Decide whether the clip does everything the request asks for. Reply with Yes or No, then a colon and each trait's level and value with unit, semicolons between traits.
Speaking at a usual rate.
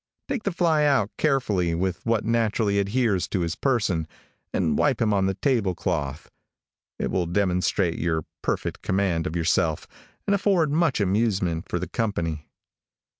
Yes: average, 155 wpm